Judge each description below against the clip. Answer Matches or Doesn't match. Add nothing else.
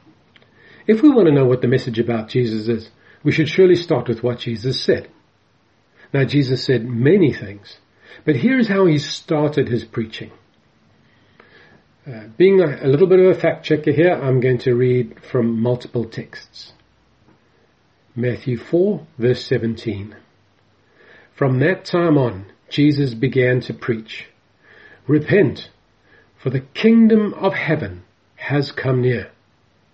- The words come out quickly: Doesn't match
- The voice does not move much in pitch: Doesn't match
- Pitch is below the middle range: Matches